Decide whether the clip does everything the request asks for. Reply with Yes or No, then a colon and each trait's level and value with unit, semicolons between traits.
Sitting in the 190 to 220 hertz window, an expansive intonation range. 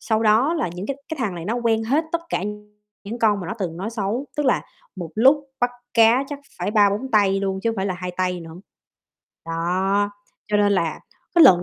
No: high, 205 Hz; average, 4.3 semitones